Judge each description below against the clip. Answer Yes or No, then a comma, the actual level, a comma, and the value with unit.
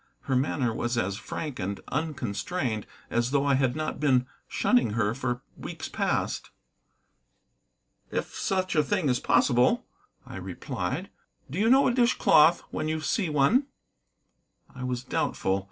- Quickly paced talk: No, average, 150 wpm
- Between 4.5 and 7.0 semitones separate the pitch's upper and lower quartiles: Yes, average, 5.2 semitones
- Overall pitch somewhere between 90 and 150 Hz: Yes, low, 135 Hz